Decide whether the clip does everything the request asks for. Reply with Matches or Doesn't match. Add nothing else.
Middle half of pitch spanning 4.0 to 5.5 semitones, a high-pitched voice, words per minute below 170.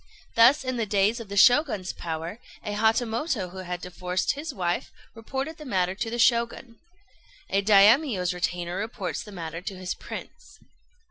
Matches